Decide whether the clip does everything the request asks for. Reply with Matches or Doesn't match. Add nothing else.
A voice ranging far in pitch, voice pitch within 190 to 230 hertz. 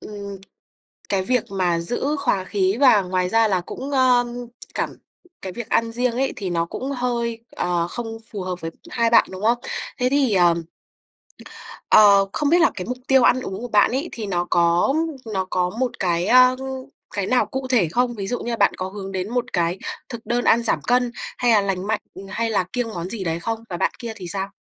Doesn't match